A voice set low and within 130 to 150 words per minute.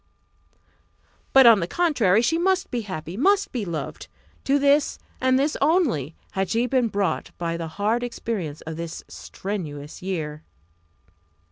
No: high, 210 Hz; average, 145 wpm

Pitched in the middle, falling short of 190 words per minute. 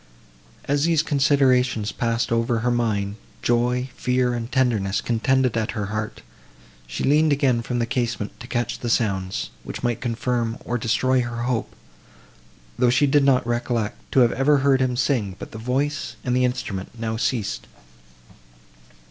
No: low, 120 Hz; average, 160 wpm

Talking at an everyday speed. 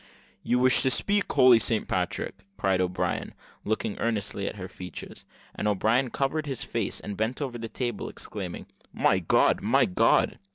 Yes: average, 165 wpm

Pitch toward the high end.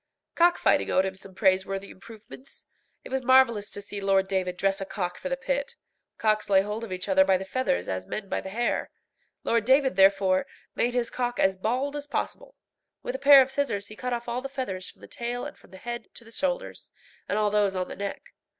Yes: high, 215 Hz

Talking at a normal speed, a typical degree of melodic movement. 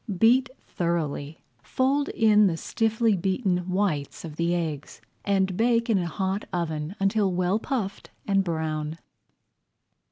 No: slow, 130 wpm; average, 4.4 semitones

